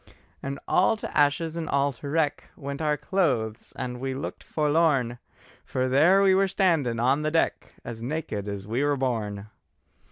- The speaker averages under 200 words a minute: Yes, average, 170 wpm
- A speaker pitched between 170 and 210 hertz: No, medium, 140 Hz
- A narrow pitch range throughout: No, average, 4.7 semitones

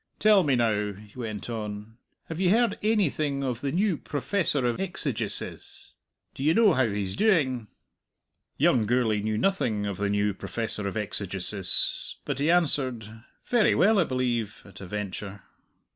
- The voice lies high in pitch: No, low, 120 Hz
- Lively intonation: Yes, wide, 7.2 semitones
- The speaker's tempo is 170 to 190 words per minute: No, average, 155 wpm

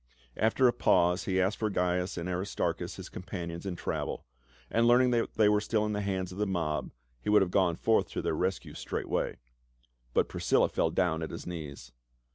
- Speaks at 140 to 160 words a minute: No, fast, 205 wpm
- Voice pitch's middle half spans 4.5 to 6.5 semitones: No, average, 3.2 semitones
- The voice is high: No, very low, 95 Hz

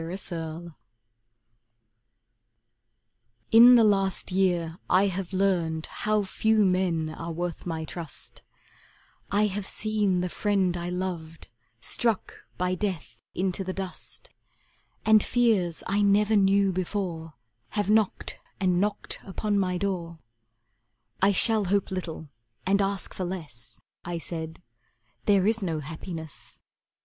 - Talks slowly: Yes, slow, 125 wpm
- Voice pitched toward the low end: No, medium, 185 Hz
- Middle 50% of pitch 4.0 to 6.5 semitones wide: No, average, 3.0 semitones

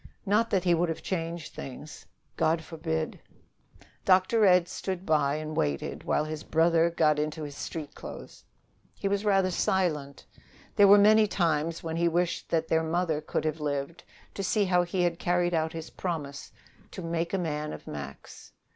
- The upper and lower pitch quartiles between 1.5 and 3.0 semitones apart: Yes, average, 2.7 semitones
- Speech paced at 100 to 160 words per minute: No, average, 175 wpm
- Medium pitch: Yes, medium, 165 Hz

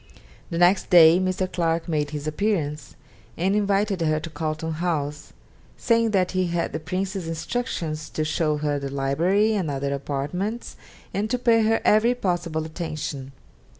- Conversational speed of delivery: Yes, average, 155 wpm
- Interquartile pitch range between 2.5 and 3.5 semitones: No, average, 4.3 semitones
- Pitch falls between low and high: Yes, medium, 170 Hz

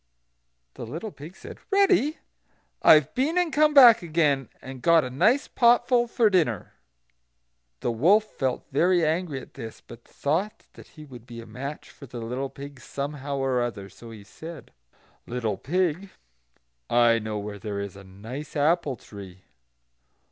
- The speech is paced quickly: No, average, 160 wpm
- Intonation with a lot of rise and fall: Yes, wide, 7.6 semitones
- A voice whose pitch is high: No, medium, 140 Hz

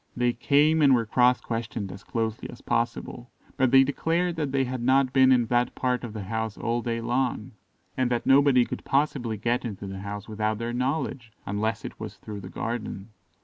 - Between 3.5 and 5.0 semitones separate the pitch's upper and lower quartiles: No, average, 3.1 semitones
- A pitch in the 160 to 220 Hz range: No, low, 120 Hz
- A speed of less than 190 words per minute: No, average, 200 wpm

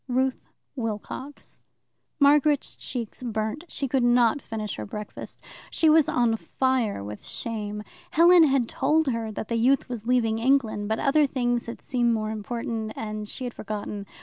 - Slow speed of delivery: No, average, 160 wpm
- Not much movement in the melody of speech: No, average, 3.6 semitones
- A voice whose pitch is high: Yes, high, 240 Hz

